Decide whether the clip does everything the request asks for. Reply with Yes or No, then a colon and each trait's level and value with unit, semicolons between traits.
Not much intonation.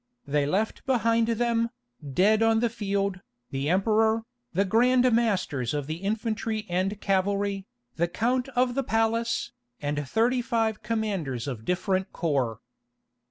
No: average, 4.3 semitones